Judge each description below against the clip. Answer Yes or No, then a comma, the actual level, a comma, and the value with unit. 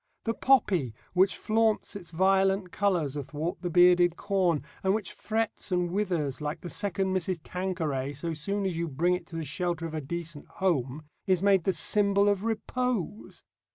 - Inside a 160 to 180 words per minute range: Yes, average, 175 wpm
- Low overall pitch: No, medium, 180 Hz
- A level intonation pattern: No, average, 3.4 semitones